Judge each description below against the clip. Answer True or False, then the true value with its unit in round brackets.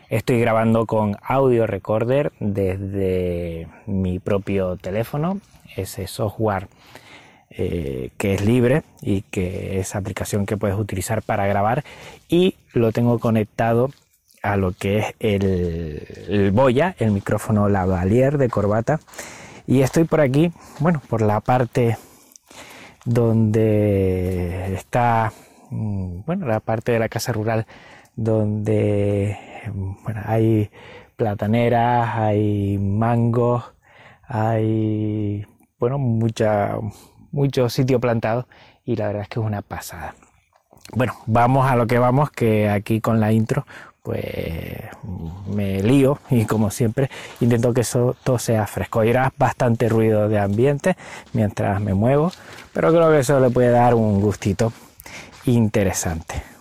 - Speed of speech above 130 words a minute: False (125 wpm)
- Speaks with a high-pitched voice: False (110 Hz)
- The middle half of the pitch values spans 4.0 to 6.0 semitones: False (3.3 semitones)